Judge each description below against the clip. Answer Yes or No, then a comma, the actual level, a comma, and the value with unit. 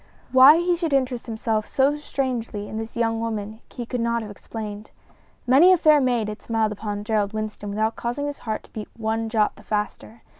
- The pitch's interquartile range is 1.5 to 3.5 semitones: Yes, average, 3.1 semitones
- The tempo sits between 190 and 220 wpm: Yes, average, 200 wpm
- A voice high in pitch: Yes, high, 225 Hz